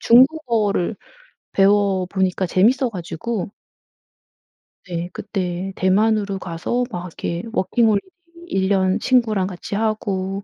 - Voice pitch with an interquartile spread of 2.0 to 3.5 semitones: Yes, average, 3.0 semitones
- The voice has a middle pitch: No, high, 195 Hz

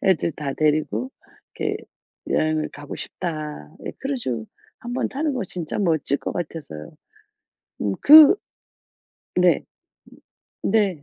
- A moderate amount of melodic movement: No, wide, 7.2 semitones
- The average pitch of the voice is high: No, medium, 160 Hz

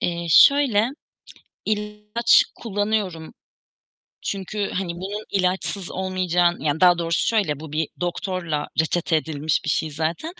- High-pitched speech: No, medium, 180 Hz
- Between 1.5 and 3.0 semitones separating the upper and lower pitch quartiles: No, average, 4.3 semitones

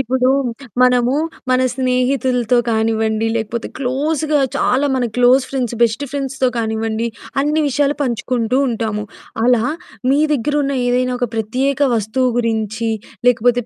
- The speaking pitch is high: Yes, very high, 250 Hz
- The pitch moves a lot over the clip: No, average, 2.9 semitones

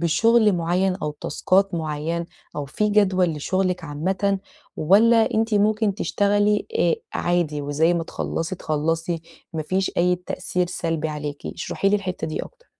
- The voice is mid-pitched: Yes, medium, 180 Hz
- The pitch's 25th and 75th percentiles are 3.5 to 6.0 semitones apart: Yes, average, 3.8 semitones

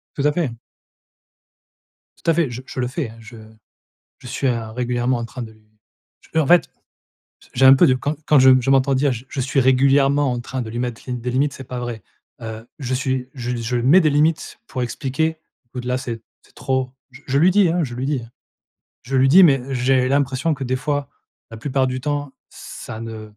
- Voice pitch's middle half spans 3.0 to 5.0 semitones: No, narrow, 2.6 semitones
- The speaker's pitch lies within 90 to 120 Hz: No, low, 130 Hz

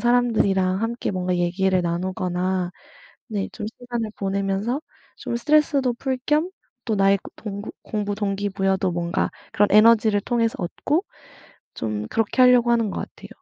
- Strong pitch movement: No, average, 4.0 semitones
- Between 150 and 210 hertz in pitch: Yes, high, 205 Hz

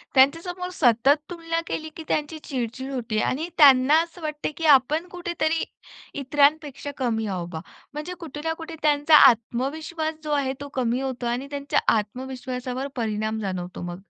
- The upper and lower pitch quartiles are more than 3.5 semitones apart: Yes, average, 4.4 semitones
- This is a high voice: Yes, very high, 275 Hz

